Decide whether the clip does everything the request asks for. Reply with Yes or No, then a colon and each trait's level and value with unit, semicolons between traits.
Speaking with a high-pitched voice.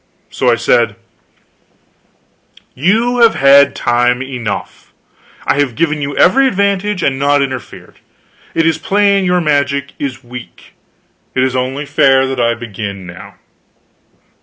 No: medium, 140 Hz